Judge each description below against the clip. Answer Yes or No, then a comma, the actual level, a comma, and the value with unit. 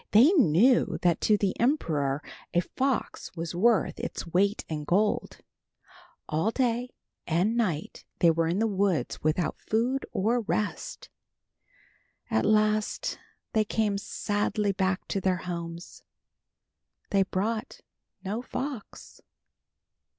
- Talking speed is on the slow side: Yes, slow, 120 wpm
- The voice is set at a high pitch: Yes, high, 205 Hz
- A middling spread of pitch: Yes, average, 4.6 semitones